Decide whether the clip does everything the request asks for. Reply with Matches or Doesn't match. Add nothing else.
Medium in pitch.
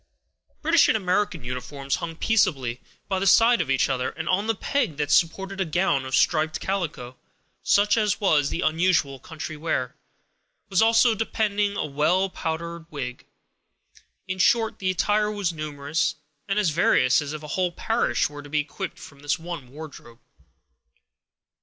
Matches